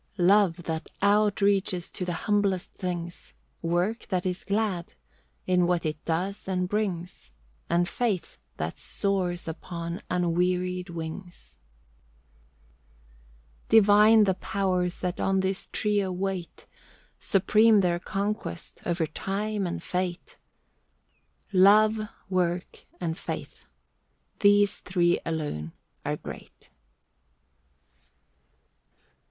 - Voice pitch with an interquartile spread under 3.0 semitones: Yes, narrow, 2.5 semitones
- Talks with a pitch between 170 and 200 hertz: Yes, medium, 185 Hz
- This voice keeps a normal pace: No, slow, 95 wpm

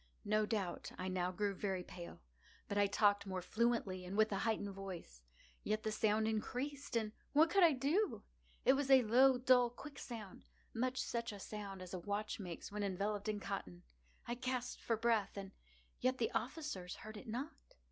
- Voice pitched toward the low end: No, high, 215 Hz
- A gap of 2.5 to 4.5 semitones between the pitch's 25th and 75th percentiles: Yes, average, 4.1 semitones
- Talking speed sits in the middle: Yes, average, 175 wpm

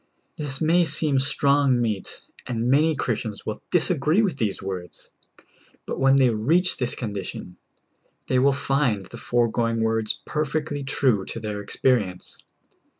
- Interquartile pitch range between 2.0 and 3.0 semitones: No, average, 4.7 semitones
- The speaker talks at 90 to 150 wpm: Yes, average, 145 wpm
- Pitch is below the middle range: Yes, low, 125 Hz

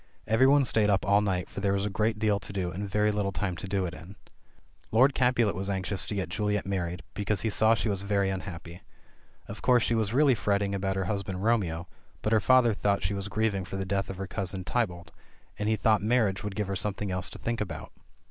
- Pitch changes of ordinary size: No, narrow, 2.1 semitones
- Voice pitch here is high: No, low, 100 Hz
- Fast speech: Yes, fast, 235 wpm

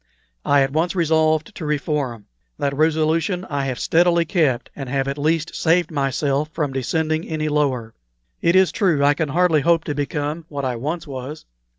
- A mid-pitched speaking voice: Yes, medium, 150 Hz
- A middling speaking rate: Yes, average, 180 wpm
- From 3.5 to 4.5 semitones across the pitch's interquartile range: No, average, 2.8 semitones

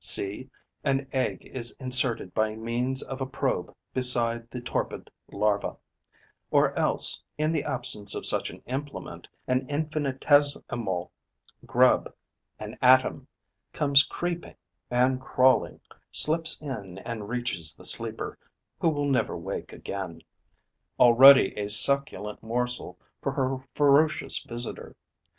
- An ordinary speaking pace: No, slow, 120 wpm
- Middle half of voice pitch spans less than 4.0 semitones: Yes, average, 3.2 semitones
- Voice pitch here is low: Yes, low, 130 Hz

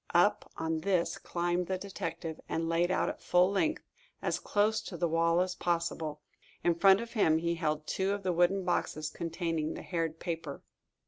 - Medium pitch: Yes, medium, 170 Hz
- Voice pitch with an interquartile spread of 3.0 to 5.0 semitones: No, narrow, 2.4 semitones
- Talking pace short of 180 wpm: No, average, 185 wpm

